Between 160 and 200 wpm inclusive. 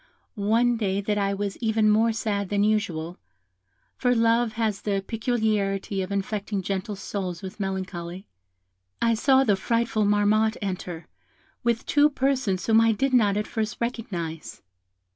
No: average, 145 wpm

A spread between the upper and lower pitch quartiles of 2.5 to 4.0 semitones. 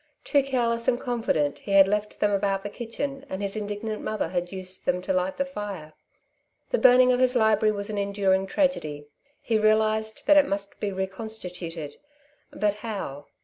Yes: average, 3.3 semitones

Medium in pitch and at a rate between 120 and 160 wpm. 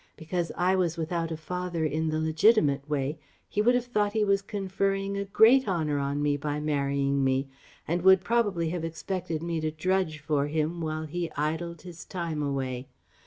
No: medium, 165 Hz; average, 185 wpm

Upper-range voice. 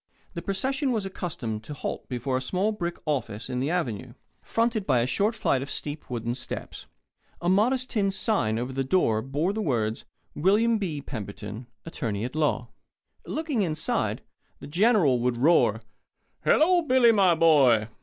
No: medium, 155 Hz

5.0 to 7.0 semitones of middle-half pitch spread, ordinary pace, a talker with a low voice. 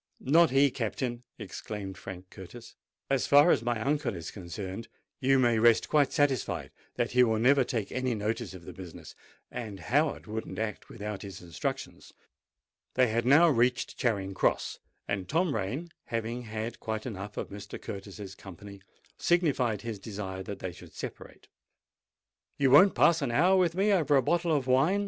Yes: wide, 5.4 semitones; average, 170 wpm; low, 120 Hz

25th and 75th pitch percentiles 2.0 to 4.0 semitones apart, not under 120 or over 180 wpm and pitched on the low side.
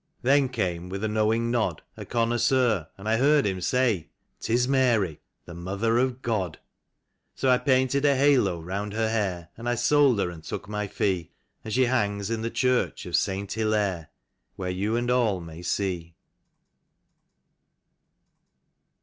No: average, 4.7 semitones; average, 160 wpm; low, 110 Hz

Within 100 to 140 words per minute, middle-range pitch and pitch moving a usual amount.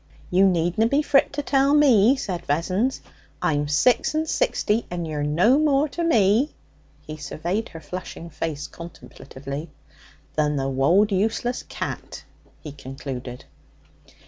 No: slow, 135 wpm; medium, 180 Hz; wide, 8.5 semitones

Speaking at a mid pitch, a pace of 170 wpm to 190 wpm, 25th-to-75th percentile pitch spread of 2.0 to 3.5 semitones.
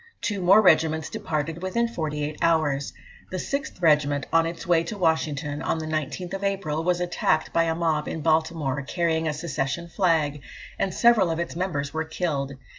Yes: medium, 160 Hz; average, 180 wpm; average, 2.7 semitones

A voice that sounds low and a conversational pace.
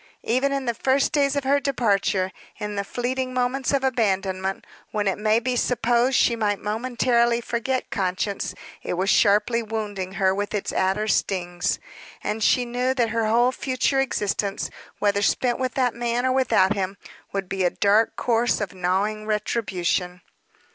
No: high, 220 Hz; average, 165 wpm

